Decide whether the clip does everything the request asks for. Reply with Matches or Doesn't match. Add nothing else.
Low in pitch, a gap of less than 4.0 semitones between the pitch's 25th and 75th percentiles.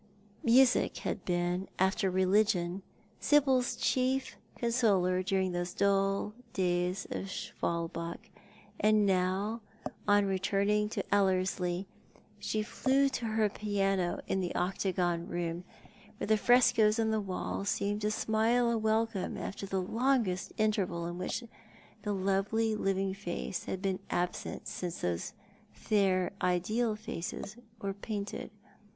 Doesn't match